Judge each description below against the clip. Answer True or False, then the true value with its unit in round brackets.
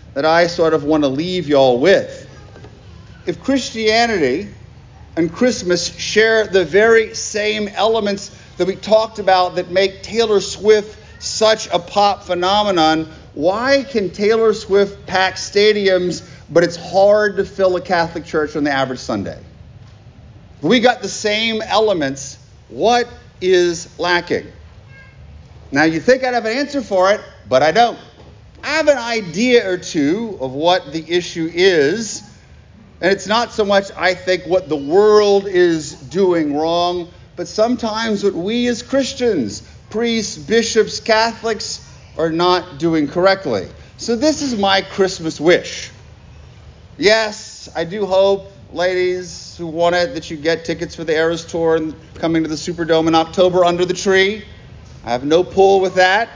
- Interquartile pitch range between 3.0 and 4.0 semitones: False (4.6 semitones)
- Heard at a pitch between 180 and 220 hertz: True (185 Hz)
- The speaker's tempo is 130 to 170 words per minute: True (155 wpm)